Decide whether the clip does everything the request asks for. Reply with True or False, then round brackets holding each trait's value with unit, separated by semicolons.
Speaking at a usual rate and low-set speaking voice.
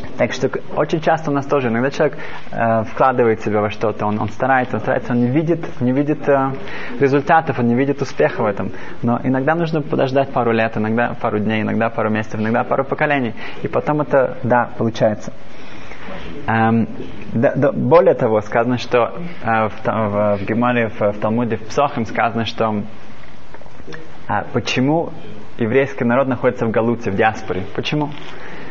False (170 wpm; 120 Hz)